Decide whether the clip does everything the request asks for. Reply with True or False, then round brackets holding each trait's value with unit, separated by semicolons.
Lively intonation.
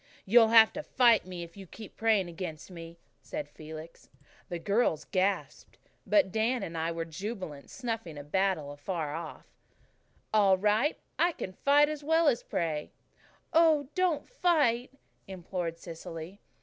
True (6.5 semitones)